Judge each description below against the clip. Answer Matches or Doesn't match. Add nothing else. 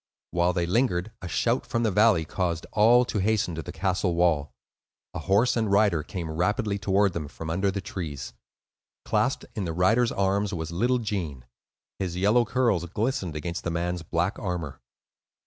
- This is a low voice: Matches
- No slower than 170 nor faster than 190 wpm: Matches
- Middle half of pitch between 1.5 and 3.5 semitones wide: Doesn't match